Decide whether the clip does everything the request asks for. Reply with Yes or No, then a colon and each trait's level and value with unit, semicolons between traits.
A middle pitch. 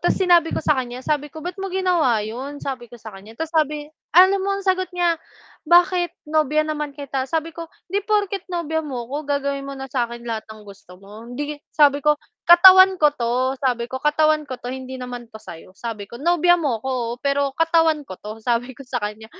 No: very high, 285 Hz